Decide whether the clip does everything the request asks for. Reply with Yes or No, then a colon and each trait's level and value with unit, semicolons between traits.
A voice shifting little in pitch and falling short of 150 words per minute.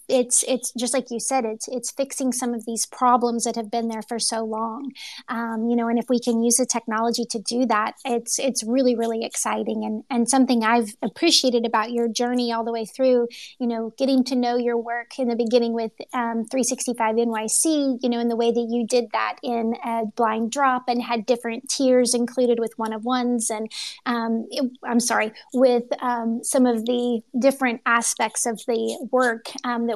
No: narrow, 1.6 semitones; fast, 205 wpm